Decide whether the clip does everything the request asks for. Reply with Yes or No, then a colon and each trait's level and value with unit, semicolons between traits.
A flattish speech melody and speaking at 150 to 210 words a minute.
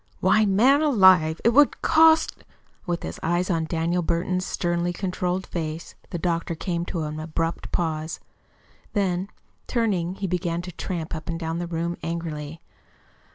Yes: narrow, 2.2 semitones; average, 155 wpm